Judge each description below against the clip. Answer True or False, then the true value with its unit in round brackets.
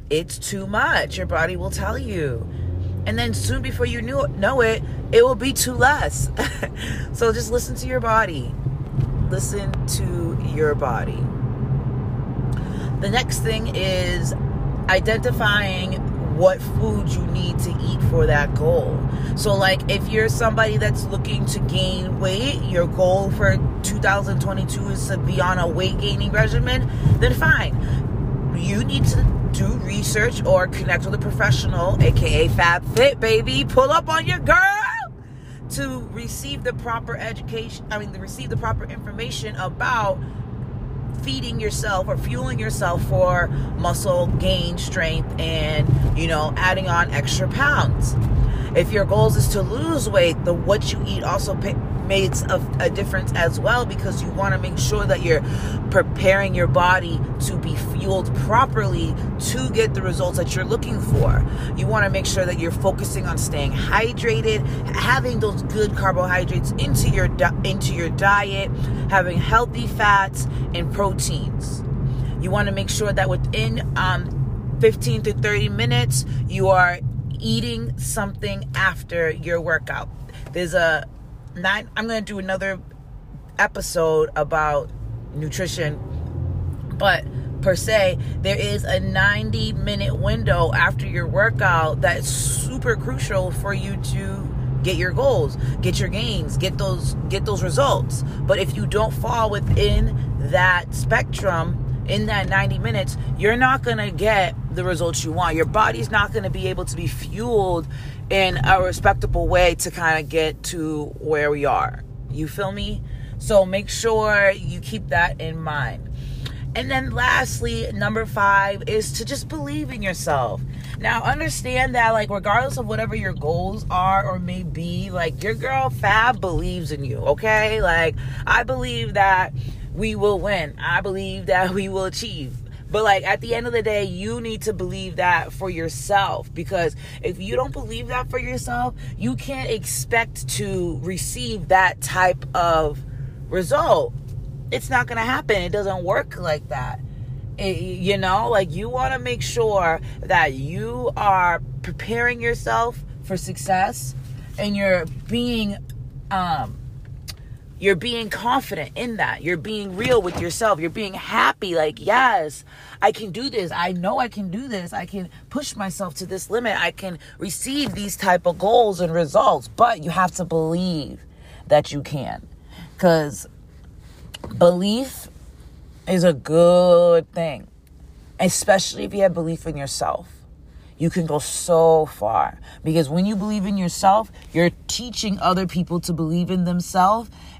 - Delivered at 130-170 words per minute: True (155 wpm)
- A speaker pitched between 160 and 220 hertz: False (135 Hz)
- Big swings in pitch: True (6.1 semitones)